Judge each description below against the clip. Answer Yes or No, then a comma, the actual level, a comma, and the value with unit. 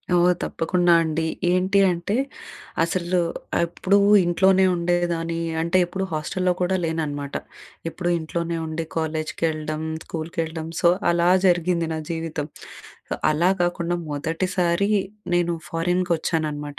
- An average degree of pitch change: No, narrow, 1.7 semitones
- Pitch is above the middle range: No, medium, 170 Hz